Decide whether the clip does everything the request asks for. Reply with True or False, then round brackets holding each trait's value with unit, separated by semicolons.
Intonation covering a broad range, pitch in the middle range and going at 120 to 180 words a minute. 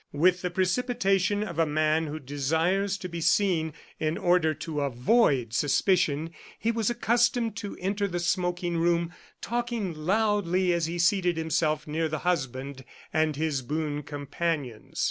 False (3.9 semitones; 170 Hz; 145 wpm)